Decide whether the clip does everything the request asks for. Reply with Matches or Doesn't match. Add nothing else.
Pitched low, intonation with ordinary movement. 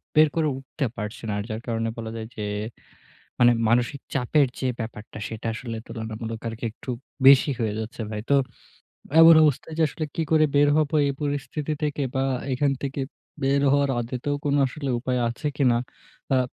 Matches